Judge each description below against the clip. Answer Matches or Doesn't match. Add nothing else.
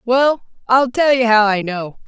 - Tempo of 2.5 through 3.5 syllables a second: Doesn't match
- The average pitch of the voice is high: Matches